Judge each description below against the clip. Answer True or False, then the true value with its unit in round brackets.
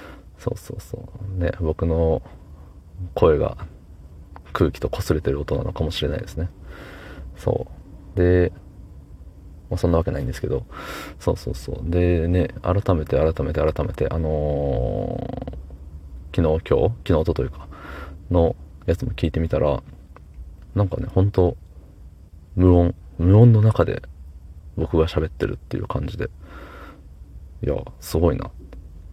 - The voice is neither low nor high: False (80 Hz)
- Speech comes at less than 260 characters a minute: True (245 characters per minute)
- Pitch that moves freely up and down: False (3.4 semitones)